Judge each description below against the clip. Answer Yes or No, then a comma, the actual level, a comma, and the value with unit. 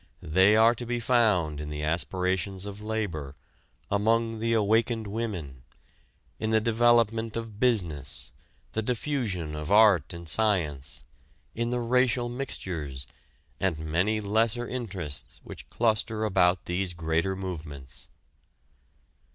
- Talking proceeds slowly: Yes, slow, 120 wpm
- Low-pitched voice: Yes, low, 100 Hz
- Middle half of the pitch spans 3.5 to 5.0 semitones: No, wide, 5.4 semitones